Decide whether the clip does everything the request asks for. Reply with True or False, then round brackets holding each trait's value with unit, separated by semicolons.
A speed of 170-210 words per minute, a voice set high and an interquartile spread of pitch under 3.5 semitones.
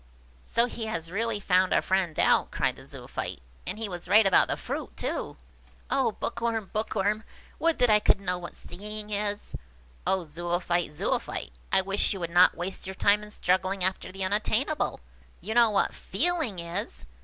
True (180 wpm; 195 Hz; 3.1 semitones)